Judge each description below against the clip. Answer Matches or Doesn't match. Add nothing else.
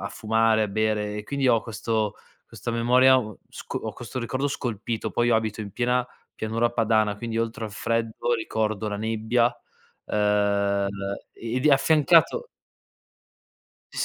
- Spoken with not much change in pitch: Matches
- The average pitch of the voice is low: Matches